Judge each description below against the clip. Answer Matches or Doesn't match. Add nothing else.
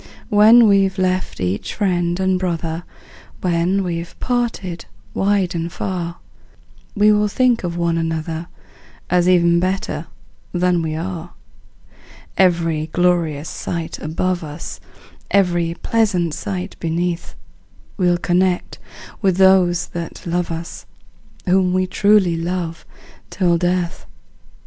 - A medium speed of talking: Doesn't match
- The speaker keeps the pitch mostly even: Matches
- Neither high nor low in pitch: Matches